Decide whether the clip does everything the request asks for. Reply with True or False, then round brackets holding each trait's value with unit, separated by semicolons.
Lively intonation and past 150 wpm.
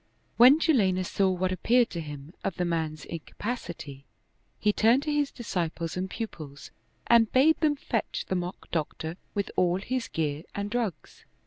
True (6.2 semitones; 165 wpm)